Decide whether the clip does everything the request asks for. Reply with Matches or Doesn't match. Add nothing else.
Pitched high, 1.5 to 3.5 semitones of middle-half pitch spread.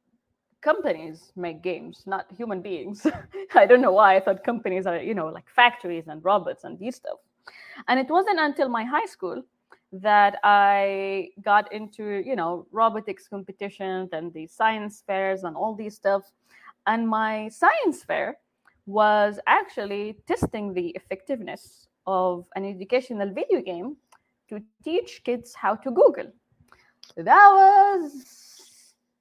Doesn't match